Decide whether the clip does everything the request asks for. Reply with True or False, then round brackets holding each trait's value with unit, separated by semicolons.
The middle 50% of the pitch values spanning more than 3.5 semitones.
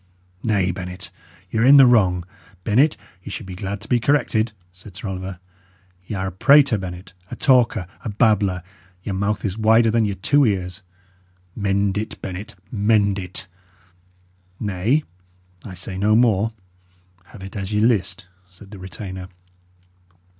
False (3.0 semitones)